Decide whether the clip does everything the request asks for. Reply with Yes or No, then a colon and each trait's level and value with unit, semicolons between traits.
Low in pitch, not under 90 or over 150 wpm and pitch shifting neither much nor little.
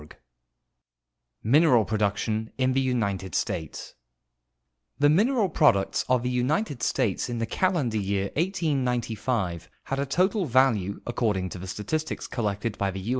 No: low, 120 Hz; average, 140 wpm; wide, 5.8 semitones